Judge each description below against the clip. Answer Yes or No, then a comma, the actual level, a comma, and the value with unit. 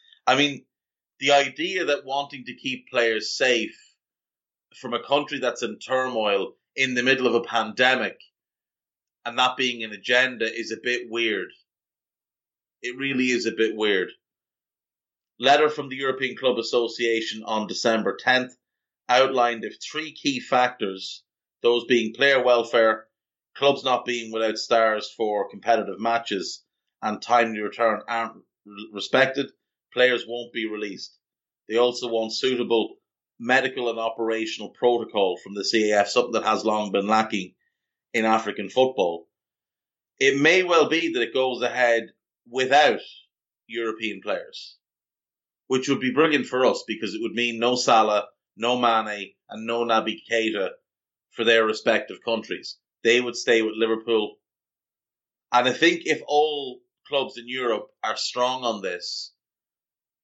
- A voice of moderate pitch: No, low, 120 Hz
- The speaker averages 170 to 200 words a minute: No, average, 140 wpm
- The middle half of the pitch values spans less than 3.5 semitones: Yes, average, 2.8 semitones